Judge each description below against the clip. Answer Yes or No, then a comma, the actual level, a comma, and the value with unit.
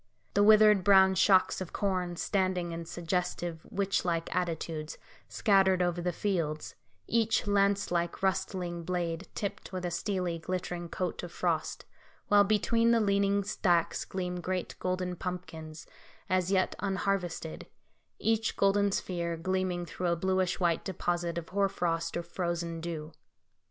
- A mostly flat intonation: Yes, narrow, 2.3 semitones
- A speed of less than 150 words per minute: Yes, average, 140 wpm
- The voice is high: No, medium, 180 Hz